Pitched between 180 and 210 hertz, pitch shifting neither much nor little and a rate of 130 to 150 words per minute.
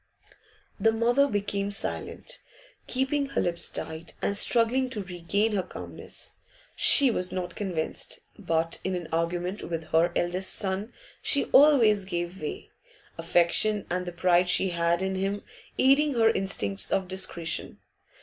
Yes: high, 190 Hz; average, 4.2 semitones; average, 140 wpm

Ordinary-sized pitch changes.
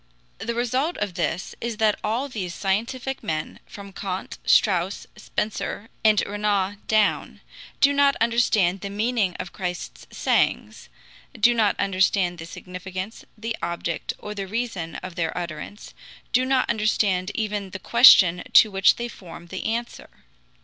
Yes: average, 3.8 semitones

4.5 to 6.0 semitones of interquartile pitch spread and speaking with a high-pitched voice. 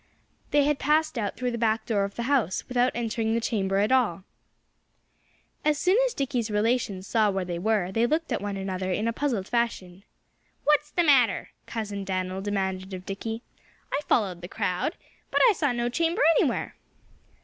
Yes: average, 4.9 semitones; high, 225 Hz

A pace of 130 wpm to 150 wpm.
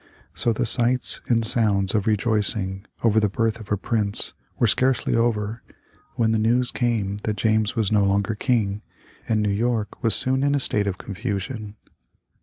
No: average, 175 wpm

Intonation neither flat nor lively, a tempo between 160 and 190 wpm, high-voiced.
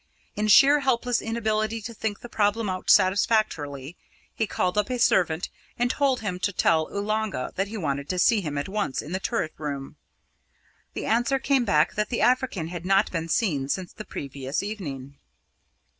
No: wide, 6.0 semitones; average, 180 wpm; high, 200 Hz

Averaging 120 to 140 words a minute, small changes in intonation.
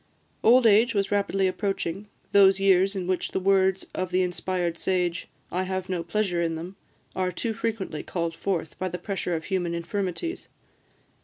No: average, 170 wpm; narrow, 1.9 semitones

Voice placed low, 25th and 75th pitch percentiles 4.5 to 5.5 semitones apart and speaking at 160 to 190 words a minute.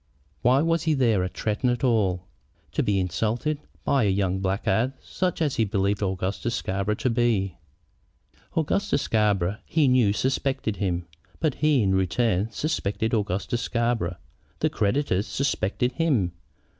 No: low, 110 Hz; average, 5.1 semitones; average, 145 wpm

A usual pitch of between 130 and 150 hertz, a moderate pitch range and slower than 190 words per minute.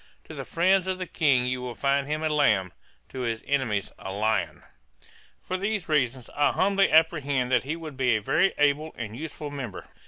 No: medium, 140 Hz; average, 4.5 semitones; average, 195 wpm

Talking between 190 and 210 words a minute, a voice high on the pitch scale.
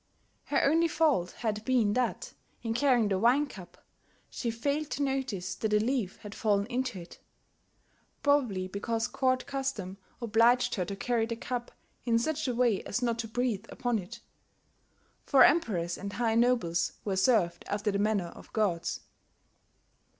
No: average, 160 wpm; high, 230 Hz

